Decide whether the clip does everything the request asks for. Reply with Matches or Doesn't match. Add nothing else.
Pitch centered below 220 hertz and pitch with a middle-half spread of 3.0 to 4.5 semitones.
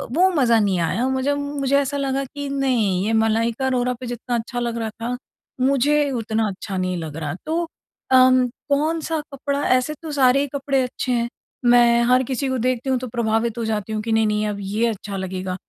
Doesn't match